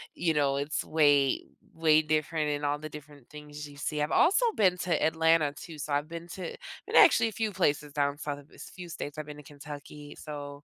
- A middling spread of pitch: No, narrow, 2.0 semitones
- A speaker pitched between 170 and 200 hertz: No, medium, 150 Hz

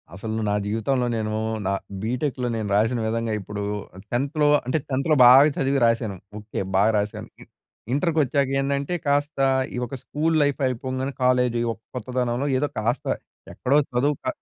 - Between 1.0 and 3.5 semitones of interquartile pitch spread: No, average, 3.9 semitones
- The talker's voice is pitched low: Yes, low, 125 Hz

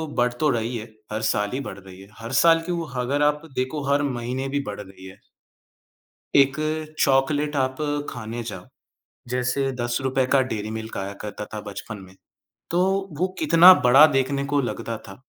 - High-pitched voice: No, low, 130 Hz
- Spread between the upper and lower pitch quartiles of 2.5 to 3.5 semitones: No, average, 4.5 semitones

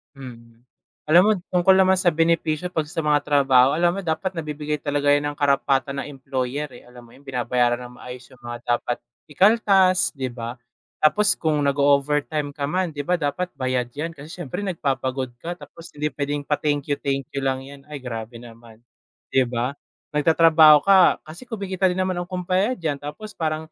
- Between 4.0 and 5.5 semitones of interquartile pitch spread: Yes, average, 4.3 semitones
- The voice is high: No, medium, 145 Hz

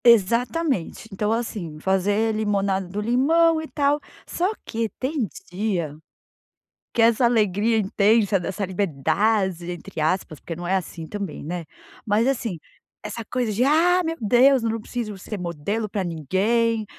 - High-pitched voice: Yes, high, 215 Hz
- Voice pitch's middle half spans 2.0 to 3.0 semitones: No, average, 4.1 semitones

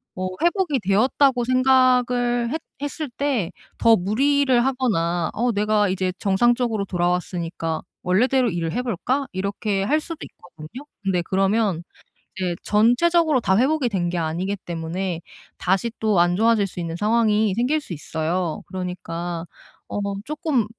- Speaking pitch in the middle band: No, high, 210 Hz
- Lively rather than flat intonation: Yes, wide, 5.9 semitones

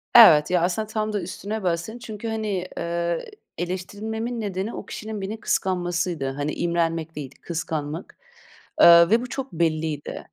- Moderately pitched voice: Yes, medium, 180 Hz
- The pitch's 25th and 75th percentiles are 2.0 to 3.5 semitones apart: No, average, 4.4 semitones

